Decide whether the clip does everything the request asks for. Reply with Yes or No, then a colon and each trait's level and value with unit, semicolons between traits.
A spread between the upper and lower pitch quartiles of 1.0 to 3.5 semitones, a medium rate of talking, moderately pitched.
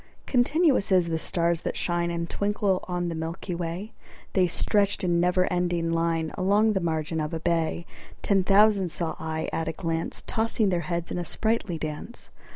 Yes: average, 3.1 semitones; average, 180 wpm; medium, 175 Hz